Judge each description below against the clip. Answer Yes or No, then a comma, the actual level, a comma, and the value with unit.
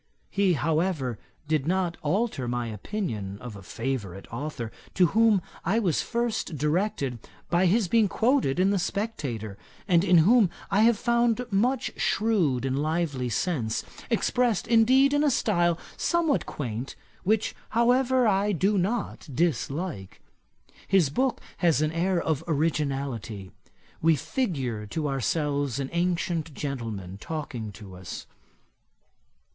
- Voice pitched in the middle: Yes, medium, 165 Hz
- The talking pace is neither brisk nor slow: No, slow, 130 wpm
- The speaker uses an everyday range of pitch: No, wide, 7.9 semitones